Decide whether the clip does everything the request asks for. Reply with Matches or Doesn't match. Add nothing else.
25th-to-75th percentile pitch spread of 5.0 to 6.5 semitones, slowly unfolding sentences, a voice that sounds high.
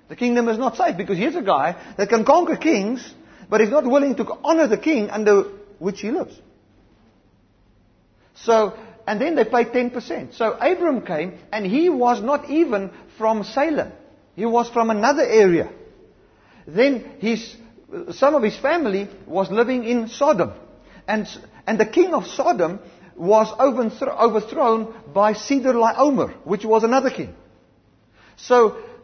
Doesn't match